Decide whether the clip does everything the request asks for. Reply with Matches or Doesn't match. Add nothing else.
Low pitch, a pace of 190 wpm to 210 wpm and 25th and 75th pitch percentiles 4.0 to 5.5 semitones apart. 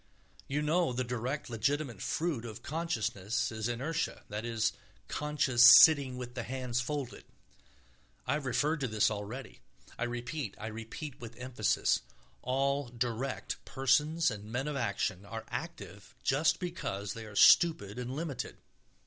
Doesn't match